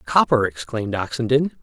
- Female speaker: No, male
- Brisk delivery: No, slow, 110 wpm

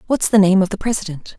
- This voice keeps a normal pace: No, fast, 260 wpm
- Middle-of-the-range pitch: No, high, 195 Hz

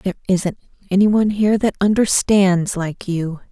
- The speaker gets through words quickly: No, slow, 135 wpm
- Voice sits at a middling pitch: No, high, 195 Hz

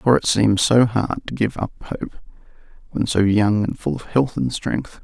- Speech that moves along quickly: Yes, fast, 215 wpm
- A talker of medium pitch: No, low, 115 Hz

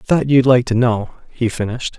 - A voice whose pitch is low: Yes, low, 120 Hz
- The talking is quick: Yes, fast, 210 wpm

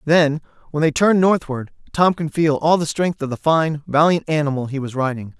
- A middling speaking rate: No, fast, 210 wpm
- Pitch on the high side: No, medium, 150 Hz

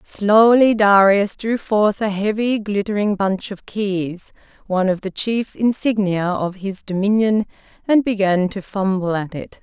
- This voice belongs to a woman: Yes, female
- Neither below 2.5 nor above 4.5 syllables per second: Yes, 4.2 syllables/s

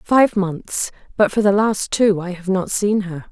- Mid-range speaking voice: No, high, 195 Hz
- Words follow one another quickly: Yes, fast, 220 wpm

